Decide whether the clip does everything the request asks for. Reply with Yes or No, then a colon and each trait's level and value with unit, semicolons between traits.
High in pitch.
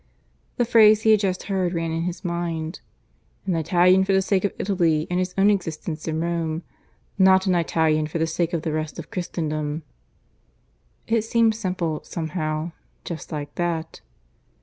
No: medium, 170 Hz